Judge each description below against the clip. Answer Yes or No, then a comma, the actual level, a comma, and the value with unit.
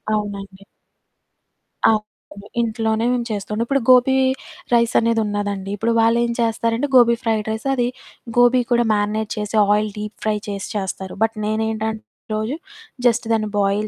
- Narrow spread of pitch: Yes, narrow, 1.9 semitones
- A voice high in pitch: Yes, high, 220 Hz